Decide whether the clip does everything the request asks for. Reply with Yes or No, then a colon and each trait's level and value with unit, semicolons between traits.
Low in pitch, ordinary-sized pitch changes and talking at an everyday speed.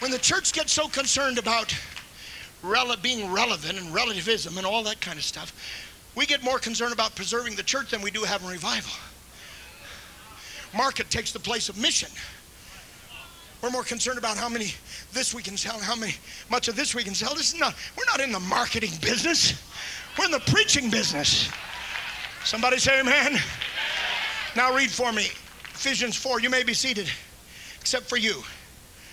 No: high, 240 Hz; average, 3.2 semitones; average, 175 wpm